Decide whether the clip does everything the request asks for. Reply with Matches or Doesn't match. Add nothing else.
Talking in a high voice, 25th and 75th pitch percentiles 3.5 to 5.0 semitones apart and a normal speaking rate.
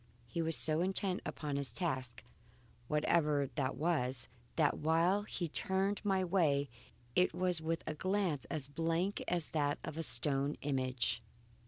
Doesn't match